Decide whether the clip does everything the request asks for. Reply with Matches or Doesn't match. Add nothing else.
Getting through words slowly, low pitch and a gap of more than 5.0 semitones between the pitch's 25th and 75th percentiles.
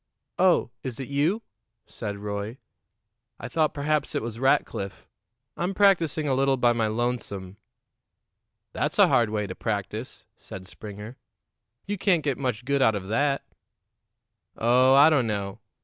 Doesn't match